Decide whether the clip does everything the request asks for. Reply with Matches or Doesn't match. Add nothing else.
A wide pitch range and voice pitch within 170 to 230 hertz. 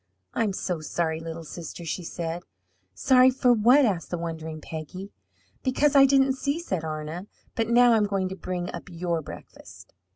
Matches